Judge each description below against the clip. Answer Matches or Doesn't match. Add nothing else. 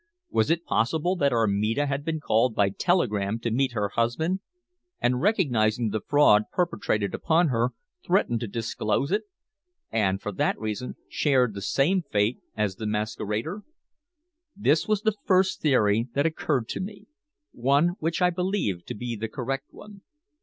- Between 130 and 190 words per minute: Matches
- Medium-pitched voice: Doesn't match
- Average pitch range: Doesn't match